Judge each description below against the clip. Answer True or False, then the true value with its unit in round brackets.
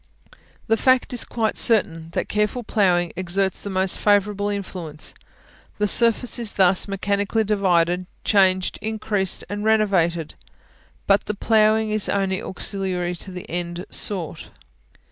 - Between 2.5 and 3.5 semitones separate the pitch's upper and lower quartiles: True (2.8 semitones)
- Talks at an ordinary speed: False (130 wpm)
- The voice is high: True (200 Hz)